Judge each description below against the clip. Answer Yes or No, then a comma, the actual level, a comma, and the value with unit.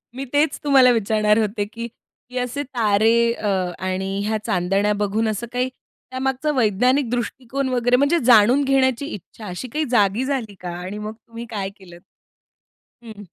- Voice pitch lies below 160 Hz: No, high, 230 Hz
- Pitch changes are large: No, average, 3.8 semitones